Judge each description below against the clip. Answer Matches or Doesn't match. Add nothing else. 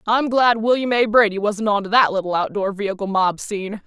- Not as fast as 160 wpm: Doesn't match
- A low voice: Doesn't match